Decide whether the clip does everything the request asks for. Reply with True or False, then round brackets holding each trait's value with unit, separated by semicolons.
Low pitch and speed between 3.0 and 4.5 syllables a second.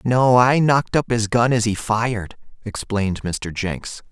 True (115 Hz; 4.4 syllables/s)